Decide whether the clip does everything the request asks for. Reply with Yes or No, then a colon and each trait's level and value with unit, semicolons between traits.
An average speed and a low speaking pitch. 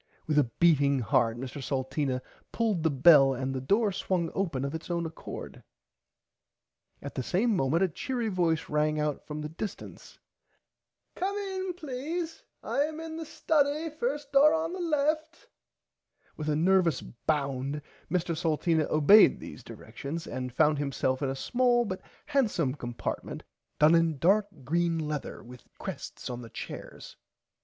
No: average, 150 wpm; medium, 165 Hz